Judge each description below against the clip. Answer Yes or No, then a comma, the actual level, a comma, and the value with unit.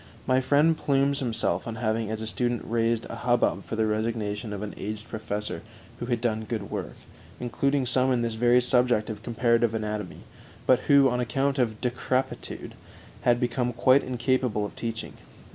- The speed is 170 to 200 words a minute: Yes, average, 175 wpm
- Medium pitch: No, low, 120 Hz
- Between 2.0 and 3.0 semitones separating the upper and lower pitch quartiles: Yes, narrow, 2.6 semitones